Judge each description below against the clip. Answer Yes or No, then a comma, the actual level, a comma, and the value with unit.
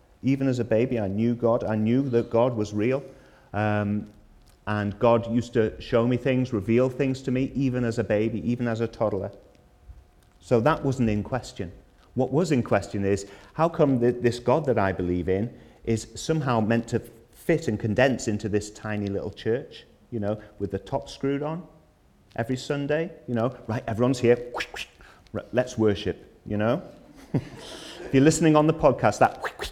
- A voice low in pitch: Yes, low, 115 Hz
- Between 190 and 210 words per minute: No, average, 180 wpm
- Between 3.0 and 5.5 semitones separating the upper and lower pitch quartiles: Yes, average, 3.6 semitones